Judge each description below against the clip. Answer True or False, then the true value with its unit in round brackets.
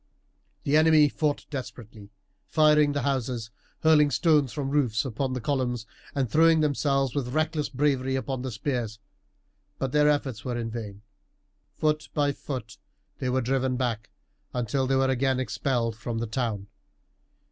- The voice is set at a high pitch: False (130 Hz)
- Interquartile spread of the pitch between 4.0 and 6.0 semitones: False (3.3 semitones)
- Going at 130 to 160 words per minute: True (155 wpm)